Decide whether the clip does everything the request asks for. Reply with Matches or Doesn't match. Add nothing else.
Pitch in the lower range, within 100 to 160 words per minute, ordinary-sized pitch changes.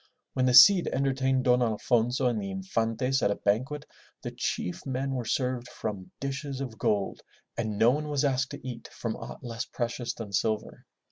Doesn't match